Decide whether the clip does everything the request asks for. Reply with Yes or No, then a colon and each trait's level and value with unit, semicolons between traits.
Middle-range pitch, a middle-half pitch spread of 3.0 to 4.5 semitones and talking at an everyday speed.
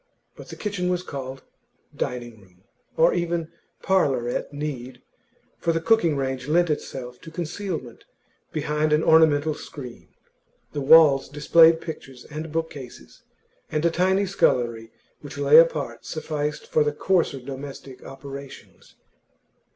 No: medium, 150 Hz; average, 3.6 semitones; slow, 130 wpm